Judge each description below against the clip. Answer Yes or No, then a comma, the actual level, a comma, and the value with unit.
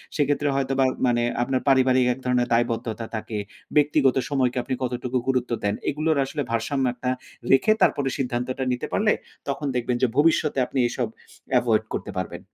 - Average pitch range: No, narrow, 2.3 semitones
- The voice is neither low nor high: No, low, 130 Hz